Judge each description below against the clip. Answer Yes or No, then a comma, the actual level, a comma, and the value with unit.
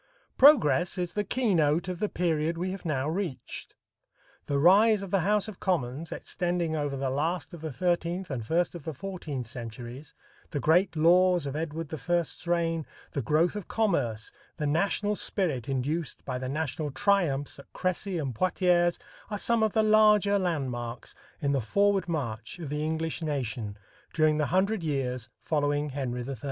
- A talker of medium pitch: Yes, medium, 160 Hz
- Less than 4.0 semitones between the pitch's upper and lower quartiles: No, average, 4.7 semitones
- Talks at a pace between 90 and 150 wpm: No, average, 170 wpm